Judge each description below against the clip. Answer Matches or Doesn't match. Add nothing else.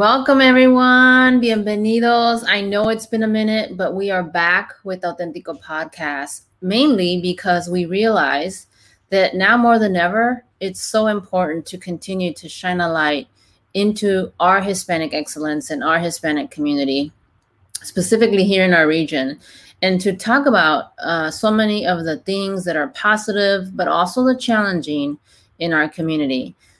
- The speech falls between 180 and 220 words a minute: Doesn't match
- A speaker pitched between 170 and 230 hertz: Matches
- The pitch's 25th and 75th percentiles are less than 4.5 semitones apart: Doesn't match